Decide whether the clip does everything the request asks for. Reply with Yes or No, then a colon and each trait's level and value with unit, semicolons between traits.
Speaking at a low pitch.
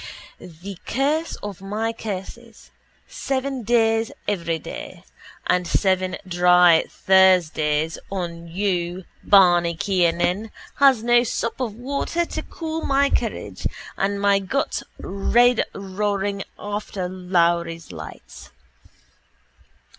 No: high, 195 Hz